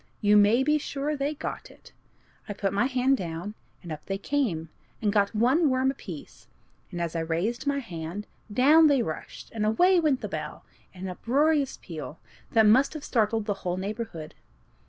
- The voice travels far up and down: Yes, wide, 6.7 semitones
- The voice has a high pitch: Yes, high, 220 Hz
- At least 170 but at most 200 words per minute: Yes, average, 185 wpm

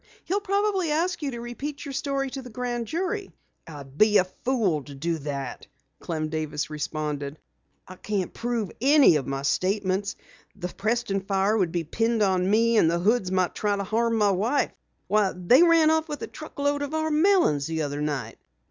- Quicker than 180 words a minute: Yes, average, 190 wpm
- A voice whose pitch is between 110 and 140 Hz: No, high, 210 Hz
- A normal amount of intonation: No, wide, 8.8 semitones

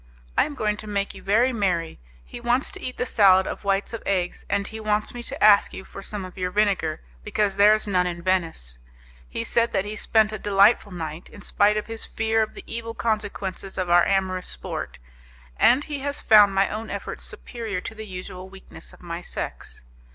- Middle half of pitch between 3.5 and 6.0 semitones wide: No, average, 2.8 semitones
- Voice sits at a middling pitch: No, high, 205 Hz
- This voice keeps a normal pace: No, fast, 215 wpm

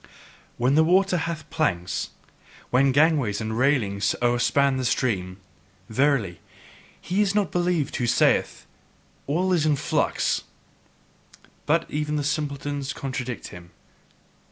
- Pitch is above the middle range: No, medium, 140 Hz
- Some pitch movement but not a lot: Yes, average, 4.7 semitones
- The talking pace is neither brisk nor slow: No, slow, 125 wpm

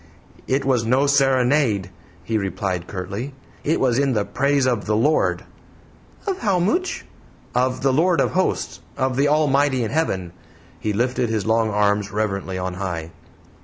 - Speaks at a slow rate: No, average, 160 wpm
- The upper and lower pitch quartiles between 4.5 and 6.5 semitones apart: Yes, wide, 5.5 semitones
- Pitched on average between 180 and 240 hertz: No, low, 125 Hz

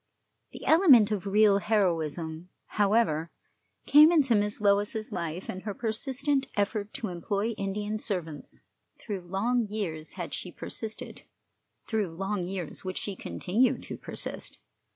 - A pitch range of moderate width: Yes, average, 3.4 semitones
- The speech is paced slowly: Yes, slow, 130 wpm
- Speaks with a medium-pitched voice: No, high, 205 Hz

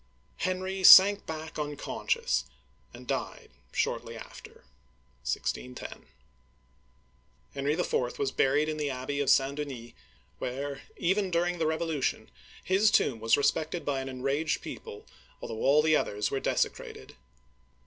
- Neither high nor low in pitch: Yes, medium, 145 Hz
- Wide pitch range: No, average, 4.1 semitones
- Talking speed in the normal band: No, slow, 130 wpm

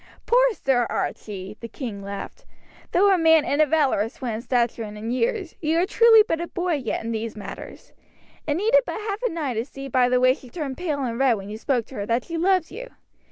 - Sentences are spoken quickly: Yes, fast, 240 wpm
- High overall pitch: Yes, very high, 275 Hz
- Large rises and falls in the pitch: Yes, wide, 7.3 semitones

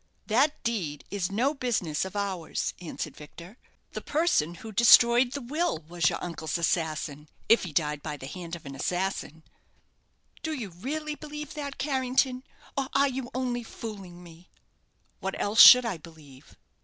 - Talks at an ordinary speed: Yes, average, 160 wpm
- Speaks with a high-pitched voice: Yes, high, 200 Hz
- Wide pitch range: Yes, wide, 7.6 semitones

